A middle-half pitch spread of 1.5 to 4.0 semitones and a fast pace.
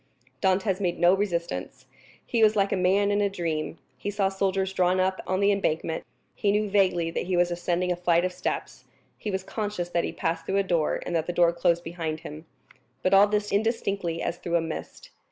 Yes: narrow, 2.6 semitones; fast, 215 wpm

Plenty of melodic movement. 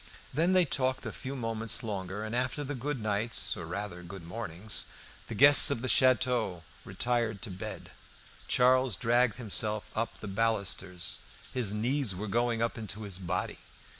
No: average, 4.1 semitones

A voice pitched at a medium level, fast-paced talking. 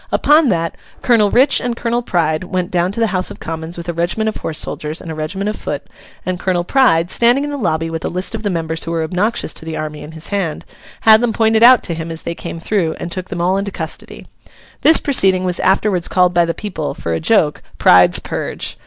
Yes: medium, 180 Hz; fast, 240 wpm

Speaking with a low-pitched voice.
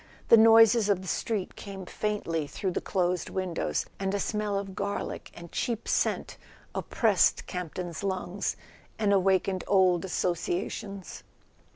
No: high, 190 Hz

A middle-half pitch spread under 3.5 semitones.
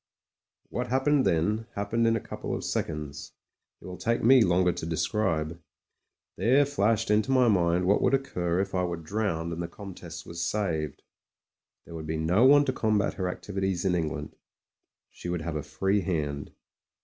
No: average, 4.7 semitones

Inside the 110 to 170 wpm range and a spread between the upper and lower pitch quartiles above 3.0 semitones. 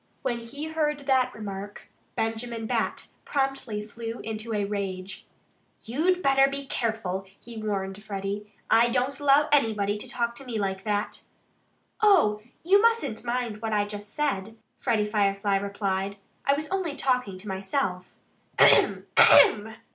Yes: average, 145 wpm; average, 4.9 semitones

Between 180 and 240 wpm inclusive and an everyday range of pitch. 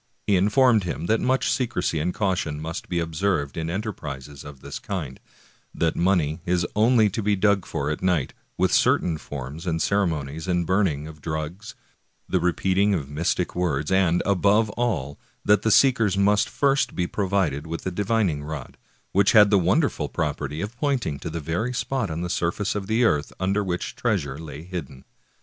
Yes: average, 185 wpm; average, 4.7 semitones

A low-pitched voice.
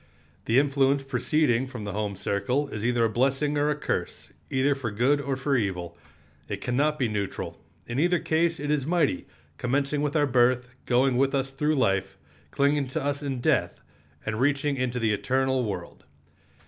Yes: low, 130 Hz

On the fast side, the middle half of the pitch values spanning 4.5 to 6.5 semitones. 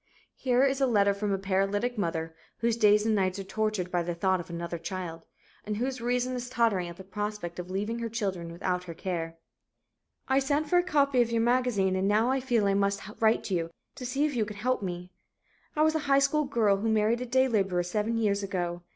Yes: fast, 225 wpm; average, 4.8 semitones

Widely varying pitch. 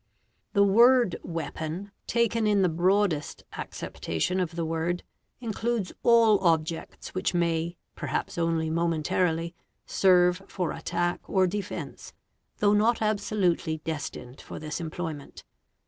No: average, 3.9 semitones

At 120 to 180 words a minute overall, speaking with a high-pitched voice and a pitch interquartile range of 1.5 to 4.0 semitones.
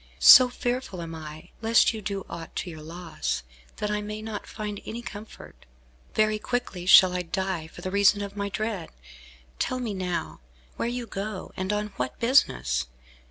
Yes: average, 170 wpm; high, 200 Hz; average, 3.7 semitones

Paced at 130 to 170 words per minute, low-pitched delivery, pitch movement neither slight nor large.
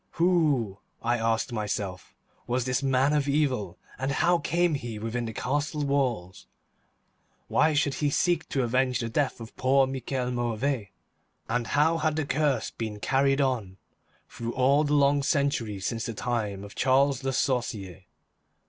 Yes: average, 155 wpm; low, 130 Hz; average, 3.8 semitones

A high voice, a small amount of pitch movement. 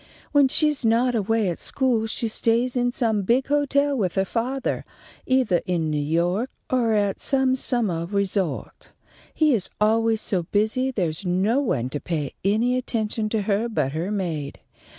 No: high, 220 Hz; average, 5.3 semitones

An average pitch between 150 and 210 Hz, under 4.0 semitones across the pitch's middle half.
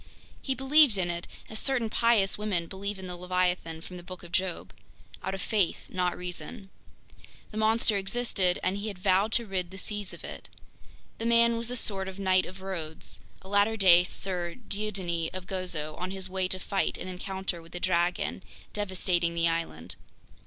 Yes: high, 190 Hz; narrow, 2.6 semitones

